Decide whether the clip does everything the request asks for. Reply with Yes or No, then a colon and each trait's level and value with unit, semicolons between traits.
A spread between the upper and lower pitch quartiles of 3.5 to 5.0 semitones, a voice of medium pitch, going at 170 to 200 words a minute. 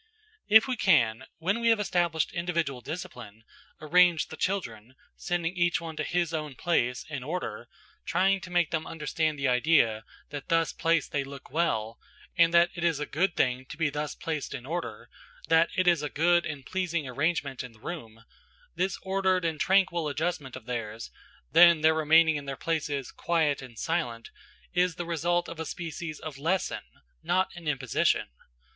Yes: average, 4.0 semitones; medium, 160 Hz; average, 175 wpm